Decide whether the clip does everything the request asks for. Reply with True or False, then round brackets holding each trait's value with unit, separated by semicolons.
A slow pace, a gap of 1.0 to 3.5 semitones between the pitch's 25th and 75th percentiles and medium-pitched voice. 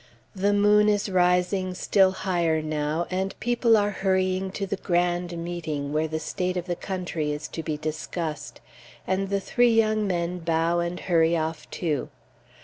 False (165 wpm; 2.9 semitones; 180 Hz)